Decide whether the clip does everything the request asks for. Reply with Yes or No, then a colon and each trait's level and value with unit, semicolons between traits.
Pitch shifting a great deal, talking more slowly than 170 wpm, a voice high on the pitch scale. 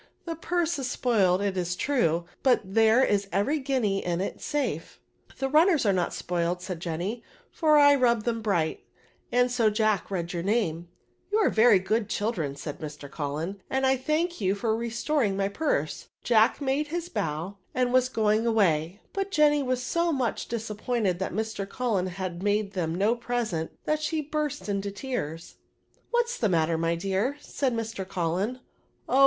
No: wide, 6.3 semitones; average, 190 wpm; high, 220 Hz